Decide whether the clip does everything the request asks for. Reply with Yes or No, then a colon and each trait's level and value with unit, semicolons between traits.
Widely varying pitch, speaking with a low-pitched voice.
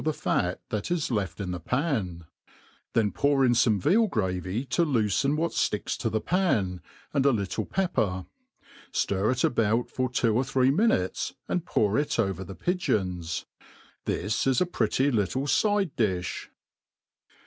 Yes: wide, 6.8 semitones; low, 115 Hz